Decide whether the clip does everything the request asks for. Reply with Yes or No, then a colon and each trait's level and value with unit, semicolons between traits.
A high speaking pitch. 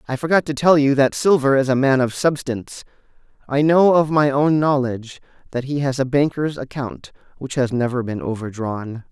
No: low, 135 Hz